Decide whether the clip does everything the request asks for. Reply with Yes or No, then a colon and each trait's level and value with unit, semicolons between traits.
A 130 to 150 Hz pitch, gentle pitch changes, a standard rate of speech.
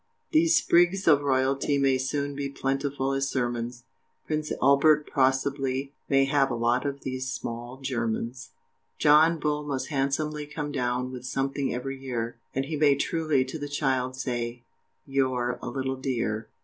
Yes: low, 135 Hz; narrow, 2.1 semitones; average, 155 wpm